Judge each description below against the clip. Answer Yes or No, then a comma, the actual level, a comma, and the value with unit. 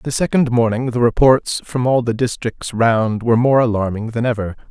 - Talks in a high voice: No, low, 120 Hz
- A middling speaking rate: Yes, average, 190 wpm